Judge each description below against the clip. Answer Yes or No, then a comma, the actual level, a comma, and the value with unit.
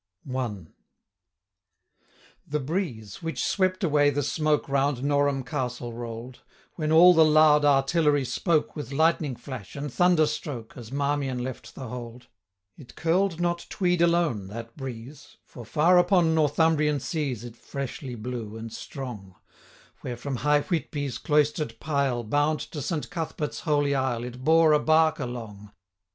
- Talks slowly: No, average, 150 wpm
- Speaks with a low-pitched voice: No, medium, 145 Hz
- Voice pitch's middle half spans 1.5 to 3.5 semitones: No, average, 4.3 semitones